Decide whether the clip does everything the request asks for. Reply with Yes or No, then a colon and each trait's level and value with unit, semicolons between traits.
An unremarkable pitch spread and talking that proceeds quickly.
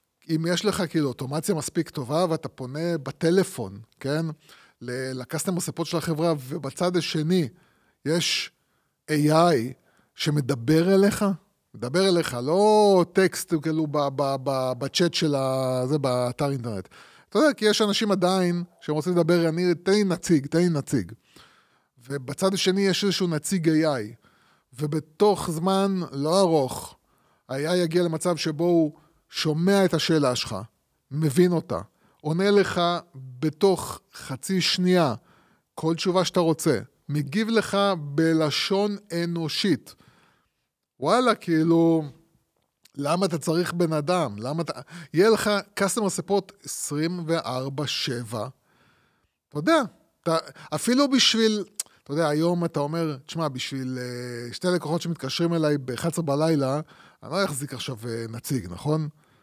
No: average, 4.1 semitones; average, 125 wpm